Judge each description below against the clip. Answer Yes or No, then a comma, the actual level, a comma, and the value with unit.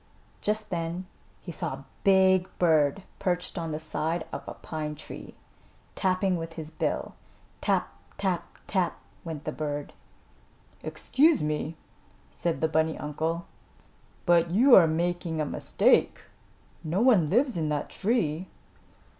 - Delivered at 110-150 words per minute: Yes, slow, 135 wpm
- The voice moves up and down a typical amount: Yes, average, 3.1 semitones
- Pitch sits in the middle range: Yes, medium, 170 Hz